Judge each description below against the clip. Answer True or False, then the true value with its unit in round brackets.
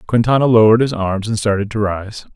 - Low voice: True (110 Hz)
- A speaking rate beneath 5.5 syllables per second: False (6.1 syllables/s)